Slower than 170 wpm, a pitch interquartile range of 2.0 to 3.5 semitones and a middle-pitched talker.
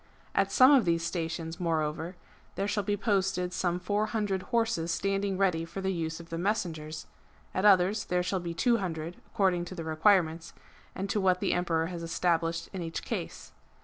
No: average, 185 wpm; average, 3.0 semitones; medium, 180 Hz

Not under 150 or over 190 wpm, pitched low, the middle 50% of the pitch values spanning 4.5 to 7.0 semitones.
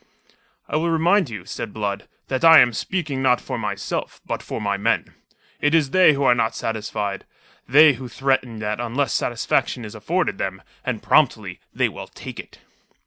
Yes: average, 180 wpm; low, 125 Hz; wide, 5.5 semitones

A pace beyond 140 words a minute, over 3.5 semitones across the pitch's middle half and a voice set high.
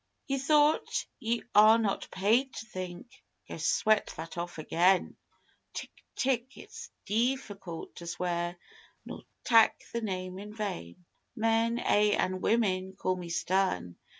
No: slow, 135 wpm; average, 4.2 semitones; high, 205 Hz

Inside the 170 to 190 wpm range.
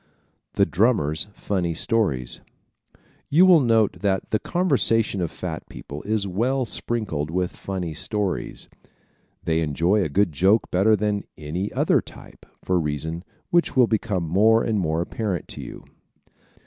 No: average, 150 wpm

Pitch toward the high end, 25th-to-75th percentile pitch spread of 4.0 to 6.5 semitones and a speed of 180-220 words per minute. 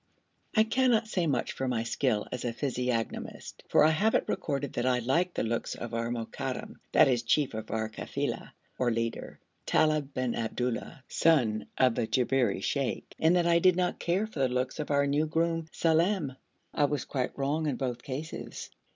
No: low, 135 Hz; average, 4.9 semitones; average, 190 wpm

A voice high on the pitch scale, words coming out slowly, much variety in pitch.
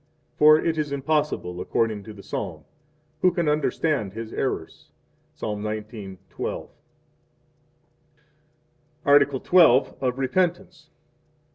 No: low, 135 Hz; slow, 100 wpm; wide, 6.4 semitones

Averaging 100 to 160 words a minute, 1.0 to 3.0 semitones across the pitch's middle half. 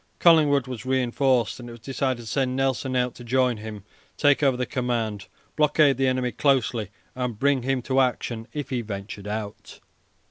No: average, 180 wpm; narrow, 2.5 semitones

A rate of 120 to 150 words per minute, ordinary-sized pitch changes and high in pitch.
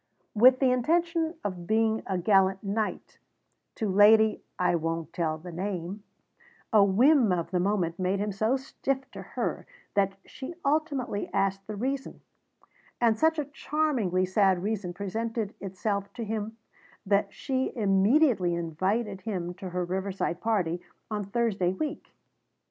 Yes: average, 145 wpm; average, 4.2 semitones; high, 205 Hz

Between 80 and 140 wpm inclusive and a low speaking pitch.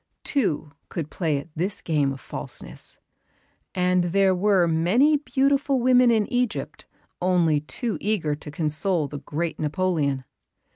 No: slow, 135 wpm; medium, 180 Hz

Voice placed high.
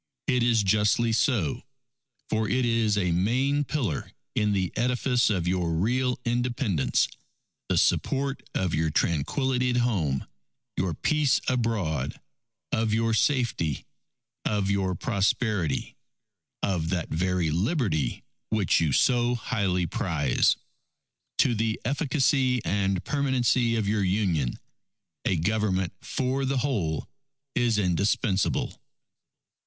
No: low, 105 Hz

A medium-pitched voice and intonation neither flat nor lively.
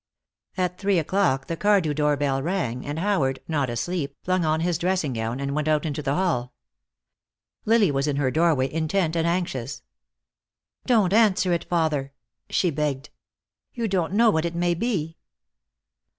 Yes: medium, 160 Hz; average, 4.6 semitones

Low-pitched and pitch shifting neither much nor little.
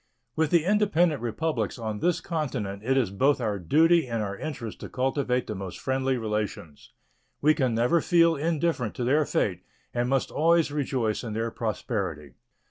No: low, 125 Hz; wide, 6.2 semitones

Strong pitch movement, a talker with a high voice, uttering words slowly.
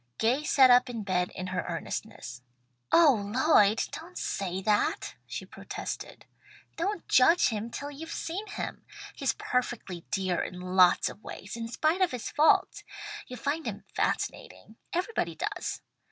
No: wide, 7.8 semitones; high, 245 Hz; average, 150 wpm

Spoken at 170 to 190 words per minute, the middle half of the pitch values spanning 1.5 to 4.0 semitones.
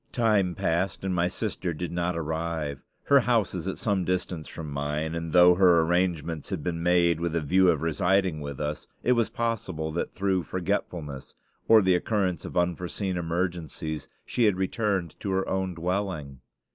Yes: average, 175 wpm; average, 2.7 semitones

